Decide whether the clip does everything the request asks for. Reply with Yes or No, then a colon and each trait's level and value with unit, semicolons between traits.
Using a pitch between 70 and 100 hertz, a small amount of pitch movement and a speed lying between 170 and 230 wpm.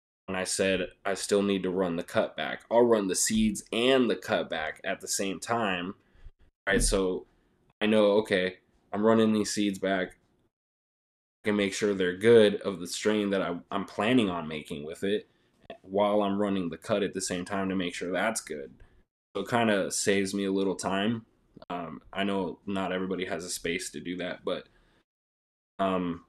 Yes: very low, 95 Hz; narrow, 2.1 semitones; average, 200 wpm